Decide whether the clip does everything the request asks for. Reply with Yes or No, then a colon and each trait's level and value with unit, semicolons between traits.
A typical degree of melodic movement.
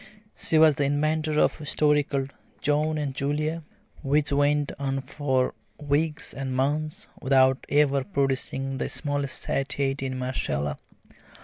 No: narrow, 1.9 semitones